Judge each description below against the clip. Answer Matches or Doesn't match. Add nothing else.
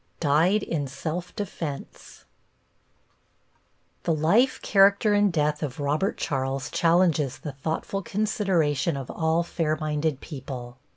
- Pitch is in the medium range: Matches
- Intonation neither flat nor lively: Matches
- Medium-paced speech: Doesn't match